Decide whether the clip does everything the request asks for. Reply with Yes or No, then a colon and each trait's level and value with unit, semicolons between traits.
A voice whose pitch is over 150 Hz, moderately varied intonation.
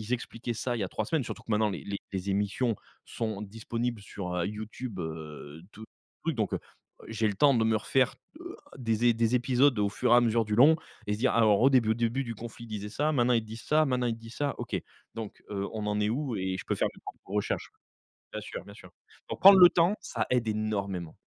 No: low, 115 Hz; average, 3.1 semitones